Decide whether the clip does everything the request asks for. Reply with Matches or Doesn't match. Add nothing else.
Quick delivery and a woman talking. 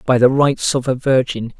Doesn't match